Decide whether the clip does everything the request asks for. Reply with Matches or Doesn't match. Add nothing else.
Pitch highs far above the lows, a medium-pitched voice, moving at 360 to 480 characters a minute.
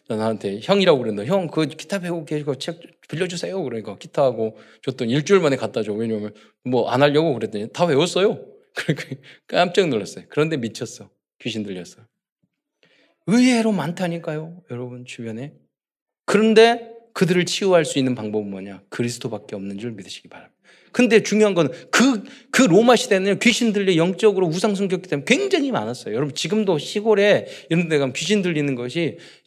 Matches